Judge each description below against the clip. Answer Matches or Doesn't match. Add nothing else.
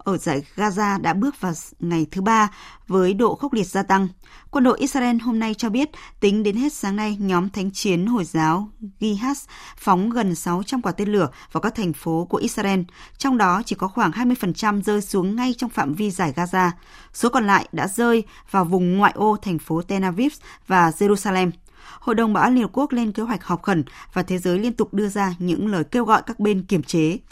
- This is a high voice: Matches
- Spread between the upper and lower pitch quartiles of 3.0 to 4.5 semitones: Matches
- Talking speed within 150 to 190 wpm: Doesn't match